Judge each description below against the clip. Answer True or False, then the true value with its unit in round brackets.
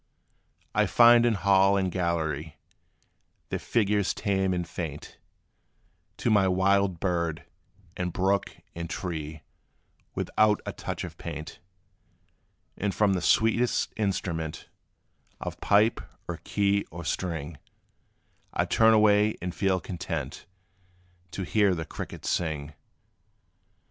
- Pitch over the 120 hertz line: False (95 Hz)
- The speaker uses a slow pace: True (120 wpm)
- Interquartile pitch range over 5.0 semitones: False (3.4 semitones)